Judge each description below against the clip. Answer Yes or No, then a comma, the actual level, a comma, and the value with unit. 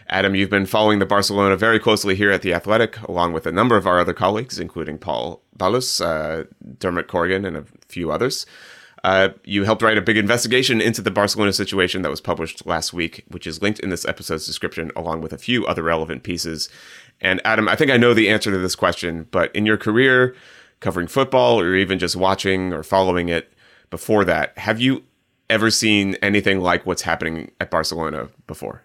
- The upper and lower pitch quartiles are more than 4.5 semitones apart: No, average, 3.7 semitones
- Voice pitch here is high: No, very low, 95 Hz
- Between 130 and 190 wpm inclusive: No, average, 200 wpm